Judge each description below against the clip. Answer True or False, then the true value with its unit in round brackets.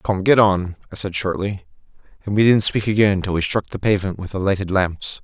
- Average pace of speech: False (230 wpm)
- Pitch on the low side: True (100 Hz)